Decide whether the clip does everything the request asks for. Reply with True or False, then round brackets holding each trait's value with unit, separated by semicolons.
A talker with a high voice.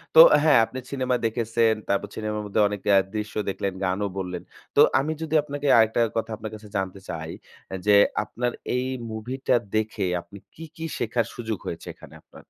False (110 Hz)